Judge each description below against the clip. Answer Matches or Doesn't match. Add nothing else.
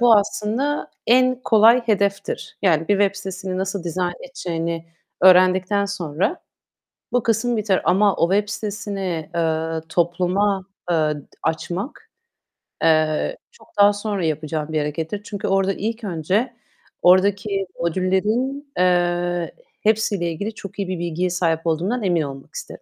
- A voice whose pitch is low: Doesn't match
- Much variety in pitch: Doesn't match